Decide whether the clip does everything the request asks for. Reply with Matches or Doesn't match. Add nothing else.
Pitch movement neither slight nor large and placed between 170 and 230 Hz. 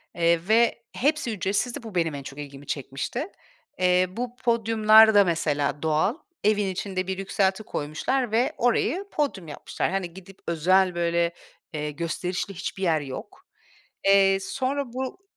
Matches